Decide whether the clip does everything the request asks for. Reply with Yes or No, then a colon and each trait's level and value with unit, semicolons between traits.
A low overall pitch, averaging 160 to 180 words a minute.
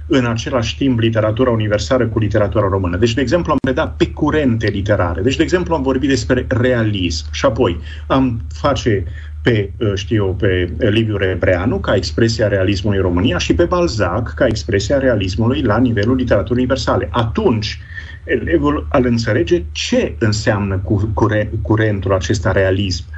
No: low, 110 Hz; average, 150 wpm